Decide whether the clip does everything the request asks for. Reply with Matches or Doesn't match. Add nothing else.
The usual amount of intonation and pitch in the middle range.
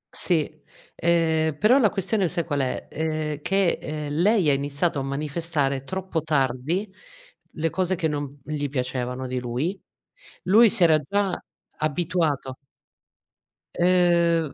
Matches